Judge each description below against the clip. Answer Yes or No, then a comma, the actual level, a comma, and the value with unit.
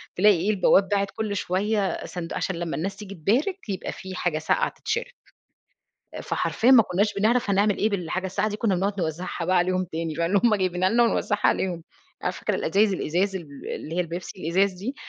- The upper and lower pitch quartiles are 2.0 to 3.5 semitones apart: Yes, average, 2.8 semitones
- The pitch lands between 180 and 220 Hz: Yes, high, 190 Hz